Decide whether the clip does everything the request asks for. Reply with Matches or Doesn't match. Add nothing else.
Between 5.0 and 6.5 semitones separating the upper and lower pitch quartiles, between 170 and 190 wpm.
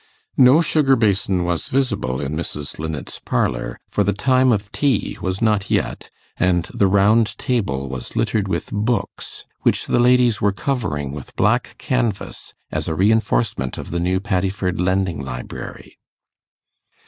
Doesn't match